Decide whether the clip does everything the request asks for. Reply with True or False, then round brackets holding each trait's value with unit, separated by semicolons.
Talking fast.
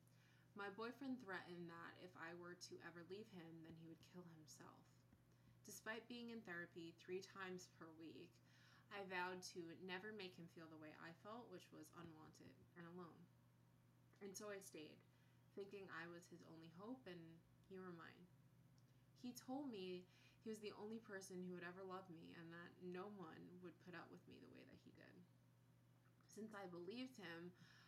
False (185 wpm)